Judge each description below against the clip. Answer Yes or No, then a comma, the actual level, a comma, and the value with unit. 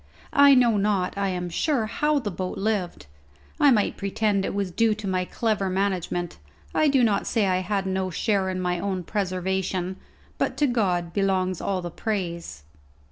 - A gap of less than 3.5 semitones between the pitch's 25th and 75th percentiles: Yes, average, 2.8 semitones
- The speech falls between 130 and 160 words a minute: No, average, 180 wpm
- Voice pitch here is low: No, high, 195 Hz